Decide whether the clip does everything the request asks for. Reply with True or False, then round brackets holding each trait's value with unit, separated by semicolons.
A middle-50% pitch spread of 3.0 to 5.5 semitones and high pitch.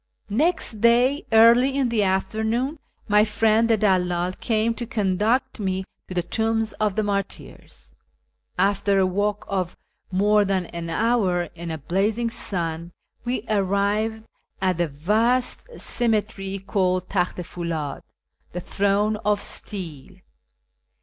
True (3.3 semitones; 205 Hz)